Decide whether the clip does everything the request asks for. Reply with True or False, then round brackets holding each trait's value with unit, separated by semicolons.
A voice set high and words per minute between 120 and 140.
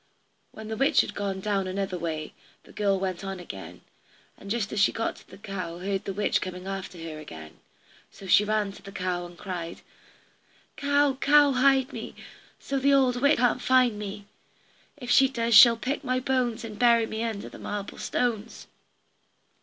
False (210 Hz; 185 wpm)